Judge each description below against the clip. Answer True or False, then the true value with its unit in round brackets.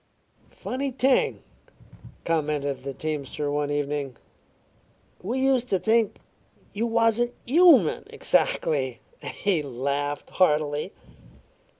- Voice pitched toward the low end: False (155 Hz)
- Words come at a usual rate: False (90 wpm)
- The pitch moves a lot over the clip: True (8.4 semitones)